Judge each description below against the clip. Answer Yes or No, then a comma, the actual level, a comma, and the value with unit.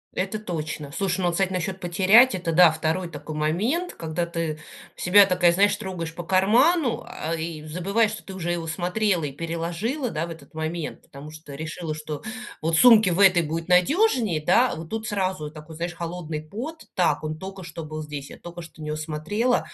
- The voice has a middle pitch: Yes, medium, 175 Hz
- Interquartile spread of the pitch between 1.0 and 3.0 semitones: No, average, 3.7 semitones